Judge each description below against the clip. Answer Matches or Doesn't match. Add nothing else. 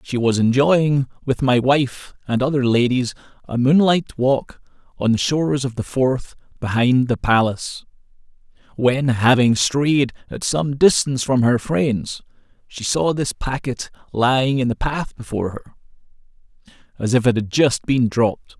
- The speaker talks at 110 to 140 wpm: Doesn't match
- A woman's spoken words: Doesn't match